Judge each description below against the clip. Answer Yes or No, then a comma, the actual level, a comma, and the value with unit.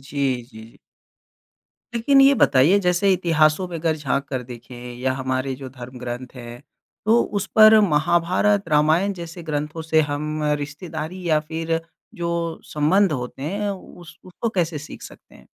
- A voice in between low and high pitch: Yes, medium, 155 Hz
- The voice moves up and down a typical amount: Yes, average, 4.6 semitones